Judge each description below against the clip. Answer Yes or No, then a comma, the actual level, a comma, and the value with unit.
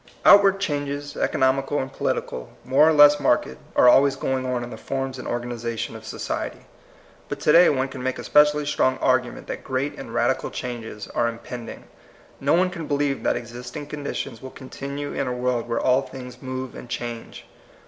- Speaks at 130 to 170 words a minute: No, average, 190 wpm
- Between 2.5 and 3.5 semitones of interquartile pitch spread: Yes, average, 2.8 semitones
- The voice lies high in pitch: No, low, 130 Hz